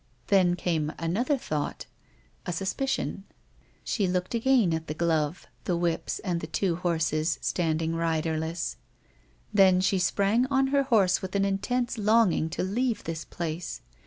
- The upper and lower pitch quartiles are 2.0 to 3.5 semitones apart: No, average, 4.2 semitones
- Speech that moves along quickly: No, average, 150 wpm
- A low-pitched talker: No, medium, 180 Hz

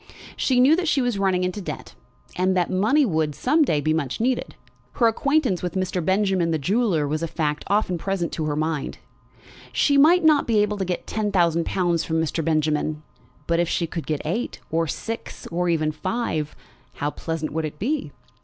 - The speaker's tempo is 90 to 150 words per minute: No, average, 200 wpm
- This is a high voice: No, medium, 180 Hz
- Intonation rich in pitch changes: Yes, wide, 5.7 semitones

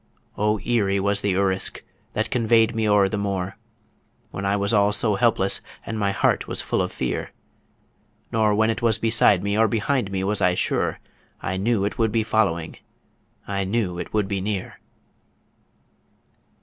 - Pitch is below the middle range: Yes, low, 105 Hz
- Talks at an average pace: Yes, average, 175 wpm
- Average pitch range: No, narrow, 2.3 semitones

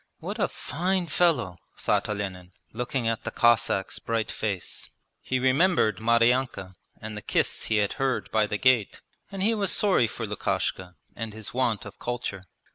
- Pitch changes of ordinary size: Yes, average, 3.8 semitones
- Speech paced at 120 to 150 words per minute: No, average, 165 wpm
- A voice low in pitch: Yes, low, 115 Hz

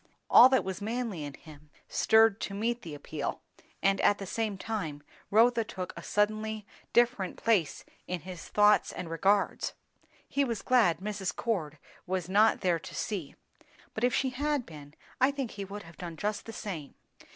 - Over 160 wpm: Yes, average, 175 wpm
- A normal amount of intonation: Yes, average, 4.5 semitones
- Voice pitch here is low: No, high, 205 Hz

